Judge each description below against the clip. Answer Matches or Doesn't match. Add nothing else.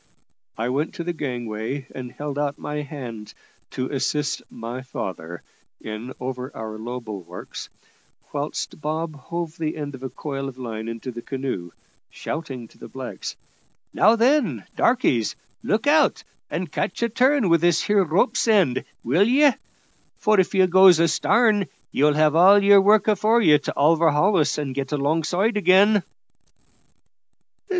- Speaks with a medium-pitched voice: Matches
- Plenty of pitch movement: Matches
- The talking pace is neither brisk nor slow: Matches